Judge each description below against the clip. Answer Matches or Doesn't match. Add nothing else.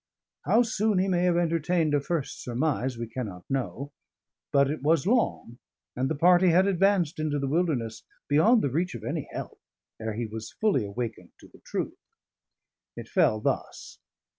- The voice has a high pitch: Doesn't match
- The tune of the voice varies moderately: Doesn't match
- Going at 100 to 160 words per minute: Doesn't match